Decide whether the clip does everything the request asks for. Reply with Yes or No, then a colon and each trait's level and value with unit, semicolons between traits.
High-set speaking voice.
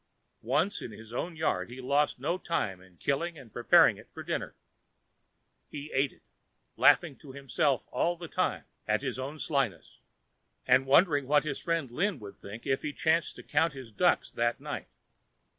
No: medium, 140 Hz